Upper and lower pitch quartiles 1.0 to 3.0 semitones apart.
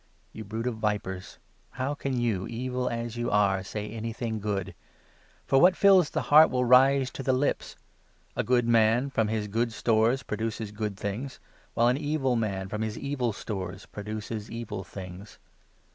No: average, 3.4 semitones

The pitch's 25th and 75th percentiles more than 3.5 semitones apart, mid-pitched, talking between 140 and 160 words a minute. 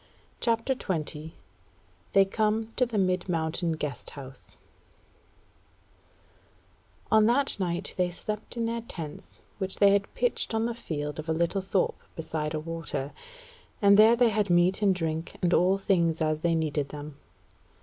Yes: average, 5.0 semitones; medium, 180 Hz; average, 155 wpm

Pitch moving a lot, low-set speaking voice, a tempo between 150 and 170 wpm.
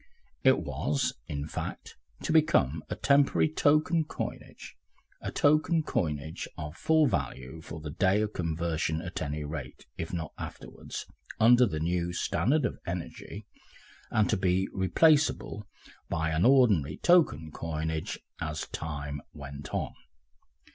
No: wide, 8.2 semitones; very low, 85 Hz; slow, 135 wpm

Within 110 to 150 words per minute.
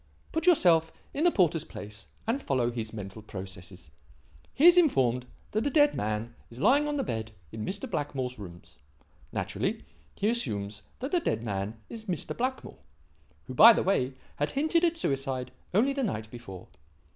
No: average, 170 wpm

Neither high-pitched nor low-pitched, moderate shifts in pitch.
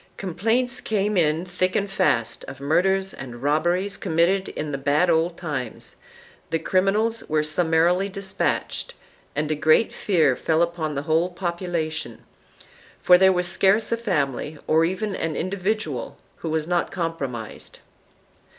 Yes: medium, 170 Hz; average, 3.7 semitones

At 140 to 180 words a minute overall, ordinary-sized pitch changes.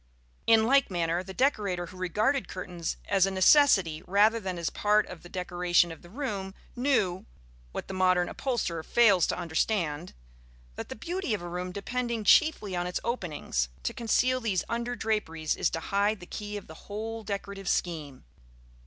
Yes: average, 175 wpm; average, 4.2 semitones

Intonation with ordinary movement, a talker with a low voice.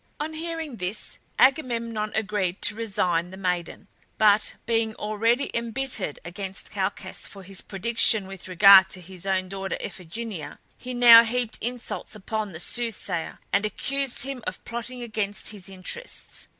No: average, 3.9 semitones; high, 215 Hz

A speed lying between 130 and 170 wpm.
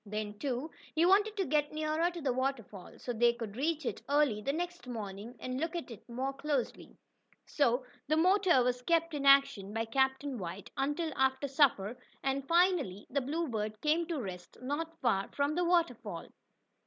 No: average, 180 wpm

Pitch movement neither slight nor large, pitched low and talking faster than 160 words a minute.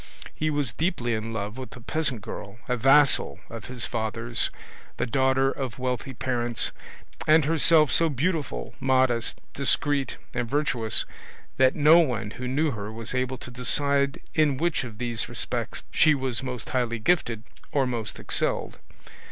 No: average, 3.6 semitones; low, 130 Hz; average, 155 wpm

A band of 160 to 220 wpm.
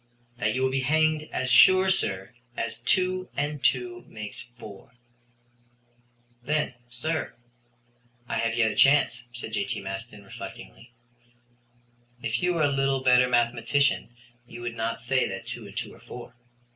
No: average, 150 wpm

